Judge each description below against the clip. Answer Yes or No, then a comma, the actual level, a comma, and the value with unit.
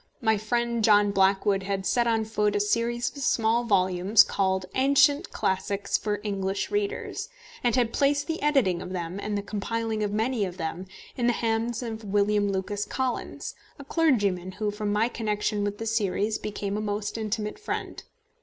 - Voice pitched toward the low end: No, high, 210 Hz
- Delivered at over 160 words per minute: Yes, average, 175 wpm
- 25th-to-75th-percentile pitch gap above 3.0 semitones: No, average, 2.7 semitones